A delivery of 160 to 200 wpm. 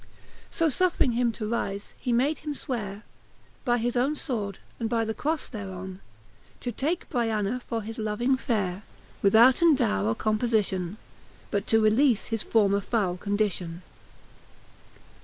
No: average, 140 wpm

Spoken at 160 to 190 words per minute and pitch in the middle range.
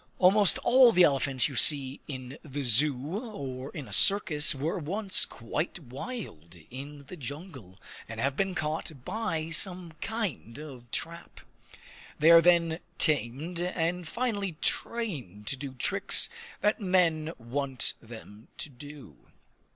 No: slow, 135 wpm; medium, 150 Hz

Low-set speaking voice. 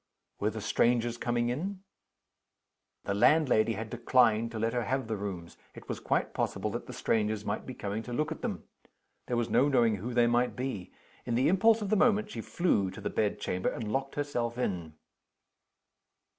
Yes: low, 120 Hz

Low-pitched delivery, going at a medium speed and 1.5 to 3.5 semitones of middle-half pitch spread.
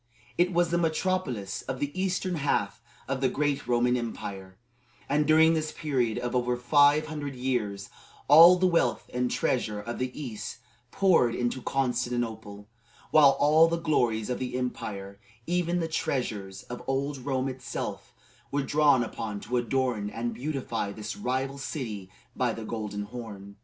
No: low, 125 Hz; average, 155 wpm; average, 4.8 semitones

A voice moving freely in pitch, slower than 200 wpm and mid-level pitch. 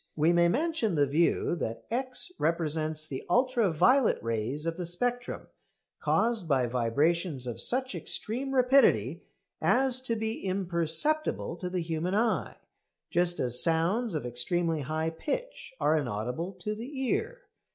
Yes: wide, 7.6 semitones; average, 140 wpm; medium, 175 Hz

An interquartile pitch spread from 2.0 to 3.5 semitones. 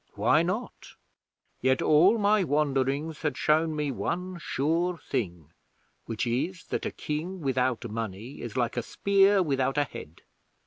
No: wide, 5.6 semitones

